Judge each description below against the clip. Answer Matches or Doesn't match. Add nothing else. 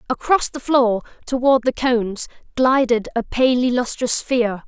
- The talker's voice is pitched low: Doesn't match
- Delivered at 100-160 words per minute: Matches